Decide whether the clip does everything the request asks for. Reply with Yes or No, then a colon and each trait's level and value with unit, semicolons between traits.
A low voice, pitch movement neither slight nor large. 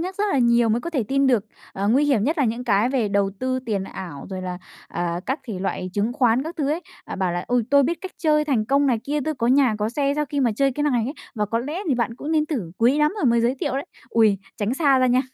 No: very high, 250 Hz; average, 4.8 semitones